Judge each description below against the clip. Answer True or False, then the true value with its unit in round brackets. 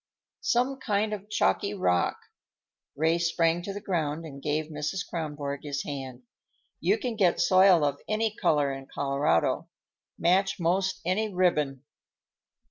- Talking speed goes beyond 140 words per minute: False (135 wpm)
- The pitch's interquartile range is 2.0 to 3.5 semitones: False (5.3 semitones)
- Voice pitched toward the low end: False (170 Hz)